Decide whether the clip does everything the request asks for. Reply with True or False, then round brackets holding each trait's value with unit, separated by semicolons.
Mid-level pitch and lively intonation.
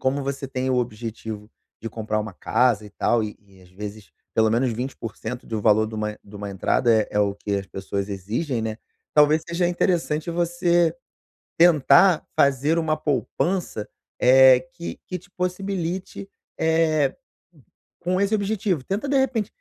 False (130 Hz; 8.0 semitones)